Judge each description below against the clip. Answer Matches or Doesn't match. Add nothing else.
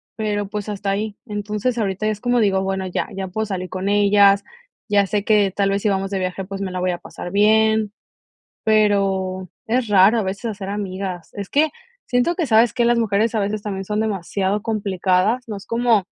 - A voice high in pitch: Matches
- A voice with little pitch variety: Matches